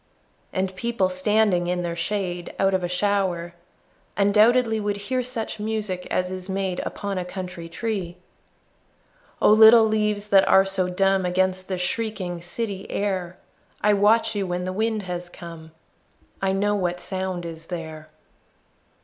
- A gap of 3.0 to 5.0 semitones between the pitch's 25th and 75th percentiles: No, narrow, 2.6 semitones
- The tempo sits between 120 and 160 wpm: Yes, average, 150 wpm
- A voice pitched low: No, high, 190 Hz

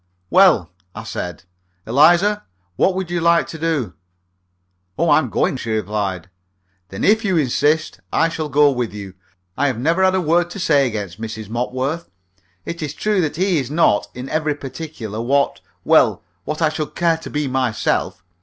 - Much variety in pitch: Yes, wide, 6.2 semitones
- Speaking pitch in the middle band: Yes, medium, 150 Hz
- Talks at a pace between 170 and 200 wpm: Yes, average, 175 wpm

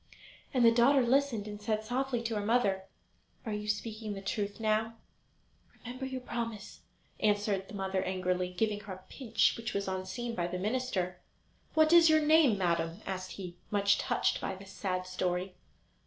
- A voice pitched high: Yes, high, 210 Hz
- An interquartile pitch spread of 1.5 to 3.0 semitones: No, average, 3.8 semitones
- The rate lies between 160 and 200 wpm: Yes, average, 170 wpm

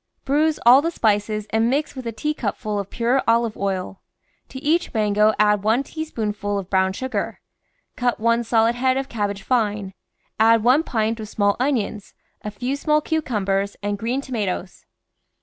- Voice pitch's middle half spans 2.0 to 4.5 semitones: Yes, average, 4.0 semitones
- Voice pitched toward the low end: No, high, 225 Hz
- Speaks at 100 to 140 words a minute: No, average, 165 wpm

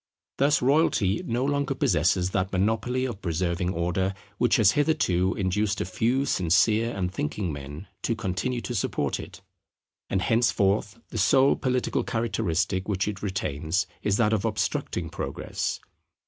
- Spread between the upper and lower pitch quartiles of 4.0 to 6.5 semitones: Yes, average, 4.4 semitones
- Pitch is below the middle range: Yes, low, 100 Hz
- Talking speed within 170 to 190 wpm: No, average, 145 wpm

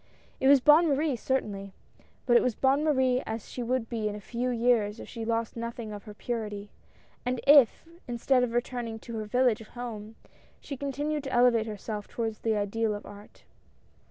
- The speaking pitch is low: No, high, 235 Hz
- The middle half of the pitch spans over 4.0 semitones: No, average, 2.9 semitones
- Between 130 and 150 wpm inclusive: No, average, 185 wpm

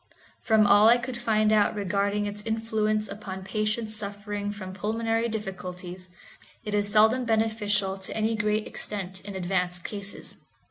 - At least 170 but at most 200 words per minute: No, average, 145 wpm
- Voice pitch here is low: No, high, 210 Hz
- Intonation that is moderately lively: No, narrow, 1.9 semitones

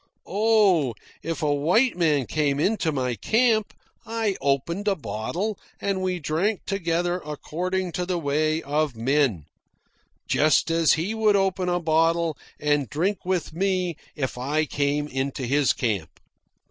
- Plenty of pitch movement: No, average, 4.6 semitones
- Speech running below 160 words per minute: Yes, average, 145 wpm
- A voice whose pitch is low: No, medium, 165 Hz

